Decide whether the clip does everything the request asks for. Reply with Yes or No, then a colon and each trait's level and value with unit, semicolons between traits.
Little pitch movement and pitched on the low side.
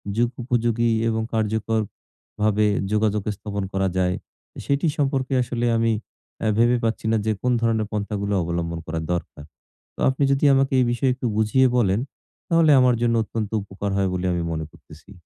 No: average, 3.3 semitones; low, 110 Hz